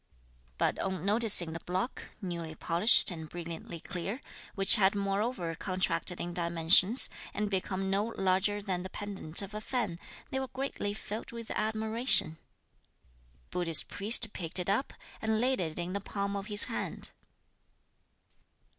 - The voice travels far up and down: No, average, 3.5 semitones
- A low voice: No, high, 195 Hz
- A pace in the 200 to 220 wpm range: No, average, 150 wpm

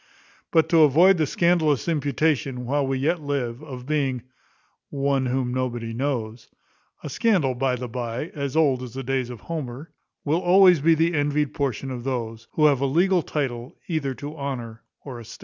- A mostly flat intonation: No, average, 3.7 semitones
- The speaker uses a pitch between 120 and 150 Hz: Yes, medium, 140 Hz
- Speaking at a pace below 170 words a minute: No, average, 180 wpm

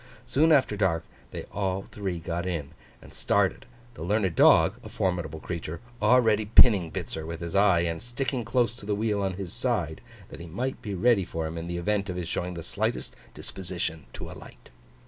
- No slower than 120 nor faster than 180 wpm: No, average, 195 wpm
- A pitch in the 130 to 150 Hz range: No, very low, 95 Hz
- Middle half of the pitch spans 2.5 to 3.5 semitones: No, average, 4.3 semitones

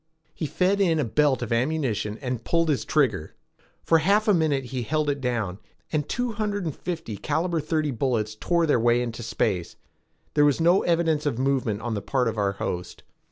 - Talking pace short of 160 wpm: No, average, 200 wpm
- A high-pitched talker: No, medium, 140 Hz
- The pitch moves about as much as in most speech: No, wide, 5.9 semitones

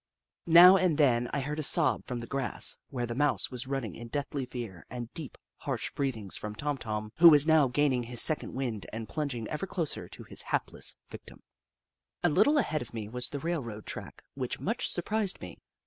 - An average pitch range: Yes, average, 4.5 semitones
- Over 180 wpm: Yes, average, 195 wpm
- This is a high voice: No, low, 135 Hz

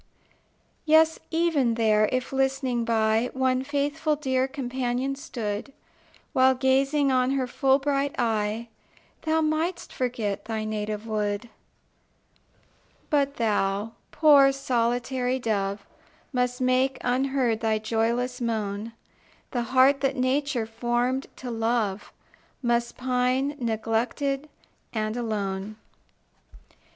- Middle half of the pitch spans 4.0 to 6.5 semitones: No, average, 3.3 semitones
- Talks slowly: Yes, slow, 105 wpm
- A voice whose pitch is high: Yes, very high, 250 Hz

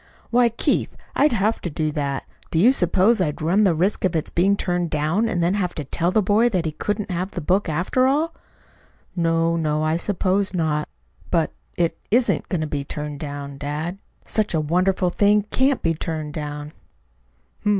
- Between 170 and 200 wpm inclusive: Yes, average, 190 wpm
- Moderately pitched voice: Yes, medium, 175 Hz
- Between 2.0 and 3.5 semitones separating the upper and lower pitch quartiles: No, average, 4.7 semitones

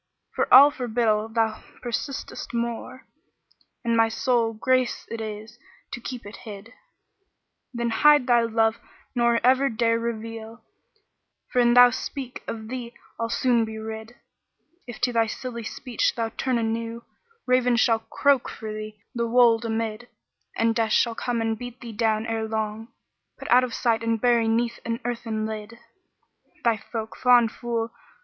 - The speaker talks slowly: No, average, 165 wpm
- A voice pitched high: Yes, high, 230 Hz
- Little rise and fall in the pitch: Yes, narrow, 1.6 semitones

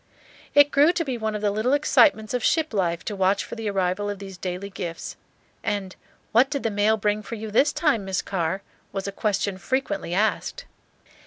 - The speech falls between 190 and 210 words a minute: Yes, average, 200 wpm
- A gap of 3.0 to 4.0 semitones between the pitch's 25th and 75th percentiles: Yes, average, 3.5 semitones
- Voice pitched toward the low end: No, high, 210 Hz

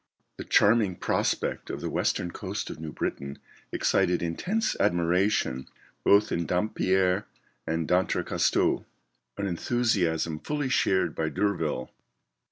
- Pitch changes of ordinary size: Yes, average, 3.7 semitones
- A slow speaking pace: Yes, slow, 115 wpm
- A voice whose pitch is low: Yes, very low, 90 Hz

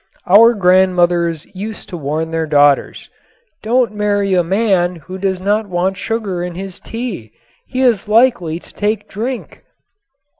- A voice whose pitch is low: No, high, 190 Hz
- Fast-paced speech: No, average, 150 wpm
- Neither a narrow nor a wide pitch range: Yes, average, 3.6 semitones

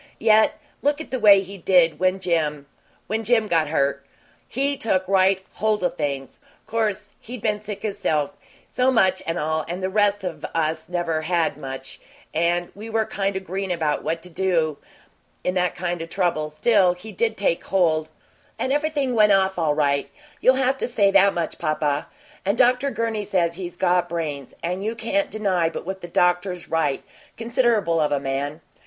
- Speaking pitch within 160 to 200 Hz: Yes, medium, 185 Hz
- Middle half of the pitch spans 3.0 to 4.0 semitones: No, average, 4.7 semitones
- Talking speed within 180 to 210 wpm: Yes, average, 185 wpm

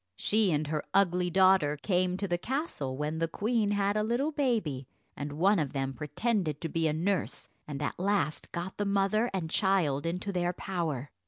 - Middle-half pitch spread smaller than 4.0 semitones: No, average, 5.0 semitones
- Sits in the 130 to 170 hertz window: No, medium, 180 Hz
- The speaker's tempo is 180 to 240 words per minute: Yes, average, 190 wpm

